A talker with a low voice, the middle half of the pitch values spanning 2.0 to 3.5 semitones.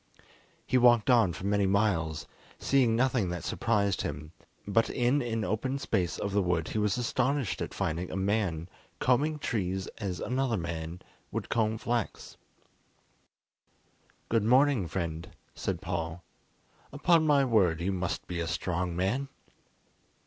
No: low, 100 Hz; wide, 5.6 semitones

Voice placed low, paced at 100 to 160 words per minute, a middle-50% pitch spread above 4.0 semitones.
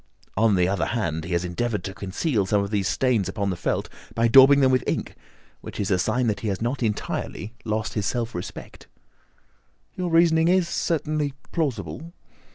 No: low, 110 Hz; average, 185 wpm; wide, 5.6 semitones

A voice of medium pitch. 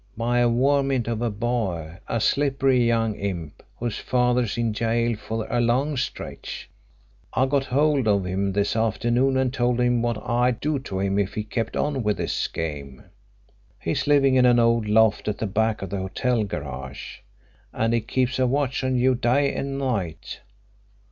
No: low, 120 Hz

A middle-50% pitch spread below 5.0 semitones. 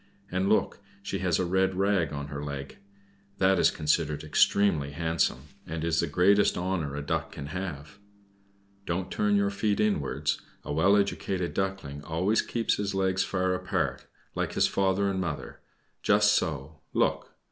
Yes: average, 4.2 semitones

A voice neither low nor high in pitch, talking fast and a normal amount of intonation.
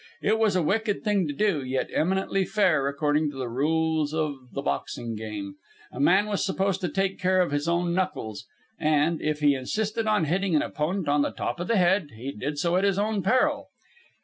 Yes: medium, 170 Hz; fast, 210 wpm; average, 5.0 semitones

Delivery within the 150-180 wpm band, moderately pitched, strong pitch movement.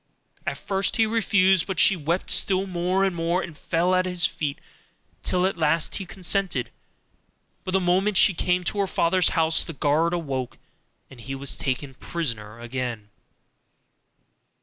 No: average, 160 wpm; medium, 175 Hz; average, 4.6 semitones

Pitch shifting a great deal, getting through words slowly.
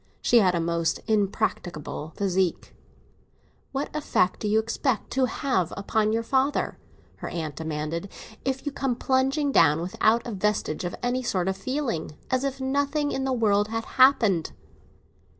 No: wide, 6.5 semitones; average, 155 wpm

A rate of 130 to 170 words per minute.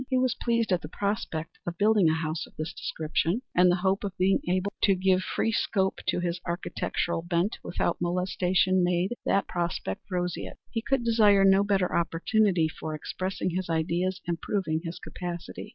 No: average, 180 wpm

